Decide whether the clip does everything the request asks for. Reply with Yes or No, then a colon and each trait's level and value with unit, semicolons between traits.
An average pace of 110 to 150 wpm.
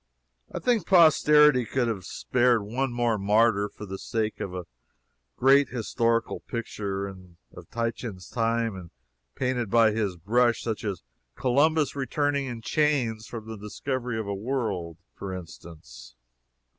Yes: average, 140 wpm